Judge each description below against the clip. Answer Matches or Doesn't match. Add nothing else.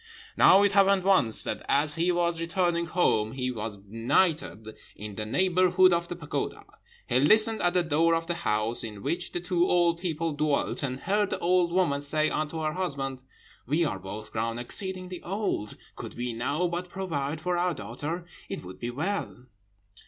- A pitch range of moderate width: Doesn't match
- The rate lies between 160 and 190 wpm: Matches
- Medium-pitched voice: Matches